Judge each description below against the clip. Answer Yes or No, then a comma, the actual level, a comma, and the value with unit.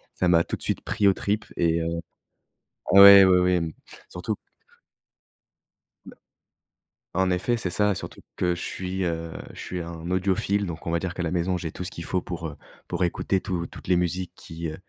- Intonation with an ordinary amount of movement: No, narrow, 1.9 semitones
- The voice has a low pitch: Yes, very low, 90 Hz